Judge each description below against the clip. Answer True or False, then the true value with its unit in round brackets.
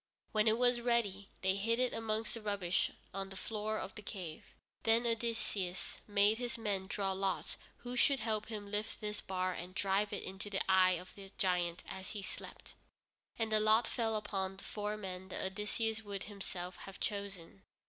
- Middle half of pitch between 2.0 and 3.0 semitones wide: True (2.5 semitones)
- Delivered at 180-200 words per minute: True (190 wpm)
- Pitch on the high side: True (205 Hz)